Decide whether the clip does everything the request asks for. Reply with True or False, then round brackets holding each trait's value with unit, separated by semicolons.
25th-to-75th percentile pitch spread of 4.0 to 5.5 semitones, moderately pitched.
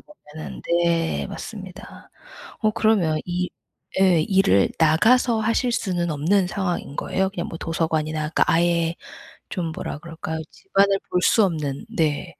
False (3.6 semitones; 175 Hz)